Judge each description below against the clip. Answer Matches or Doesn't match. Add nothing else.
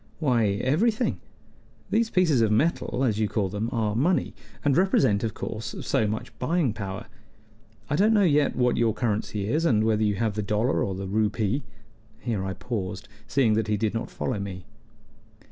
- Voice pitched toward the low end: Matches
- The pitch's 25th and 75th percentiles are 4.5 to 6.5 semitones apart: Matches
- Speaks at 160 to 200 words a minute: Matches